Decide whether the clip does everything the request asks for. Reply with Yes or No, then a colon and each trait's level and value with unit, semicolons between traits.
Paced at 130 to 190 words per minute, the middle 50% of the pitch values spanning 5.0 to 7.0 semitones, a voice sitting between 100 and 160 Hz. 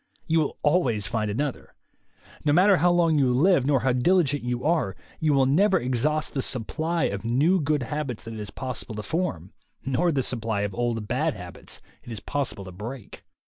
No: fast, 205 wpm; wide, 5.4 semitones; low, 135 Hz